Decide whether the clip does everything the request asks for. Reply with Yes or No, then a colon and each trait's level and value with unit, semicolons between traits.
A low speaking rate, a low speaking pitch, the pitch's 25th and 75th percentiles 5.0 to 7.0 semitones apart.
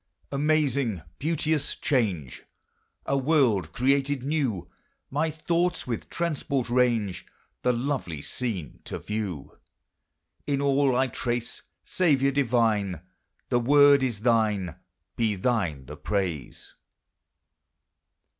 Yes: slow, 100 wpm; low, 125 Hz; average, 5.3 semitones